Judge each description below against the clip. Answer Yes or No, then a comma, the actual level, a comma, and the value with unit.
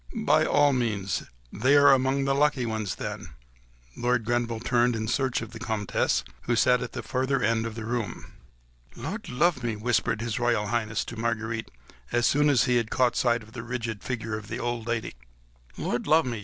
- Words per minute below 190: No, average, 195 wpm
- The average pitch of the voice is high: No, low, 120 Hz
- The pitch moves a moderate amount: No, narrow, 2.3 semitones